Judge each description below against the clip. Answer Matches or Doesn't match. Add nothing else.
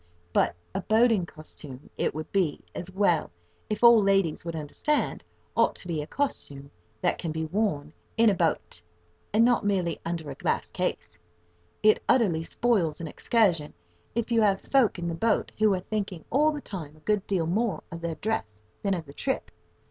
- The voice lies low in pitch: Doesn't match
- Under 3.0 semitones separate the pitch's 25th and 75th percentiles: Doesn't match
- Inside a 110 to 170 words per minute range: Doesn't match